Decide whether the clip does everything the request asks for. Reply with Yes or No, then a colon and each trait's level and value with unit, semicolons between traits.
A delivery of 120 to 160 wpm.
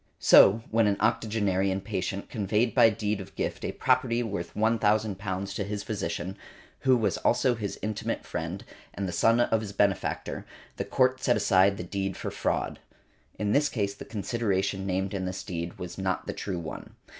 No: average, 180 wpm